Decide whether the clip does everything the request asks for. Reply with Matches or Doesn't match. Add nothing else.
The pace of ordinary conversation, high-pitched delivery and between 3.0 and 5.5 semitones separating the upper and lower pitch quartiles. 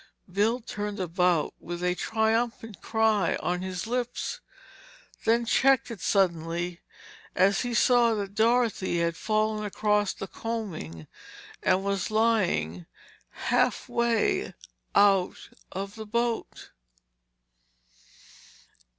Doesn't match